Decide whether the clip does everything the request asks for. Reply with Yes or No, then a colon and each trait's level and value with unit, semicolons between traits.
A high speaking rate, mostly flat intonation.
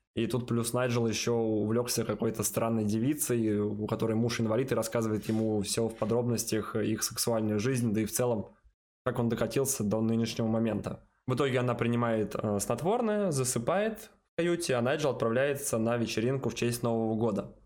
Yes: fast, 170 wpm; narrow, 2.0 semitones